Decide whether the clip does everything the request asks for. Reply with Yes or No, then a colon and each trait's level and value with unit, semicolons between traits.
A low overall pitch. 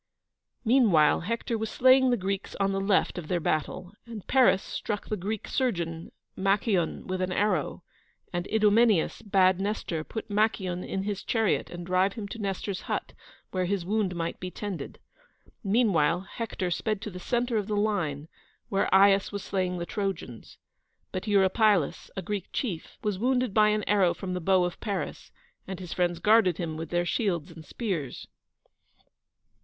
No: high, 195 Hz